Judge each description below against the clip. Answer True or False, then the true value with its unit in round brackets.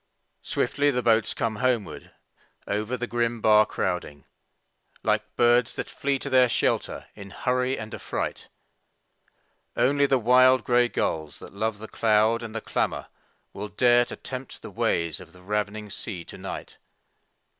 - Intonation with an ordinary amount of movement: True (3.1 semitones)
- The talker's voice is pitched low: True (115 Hz)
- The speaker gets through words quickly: False (155 wpm)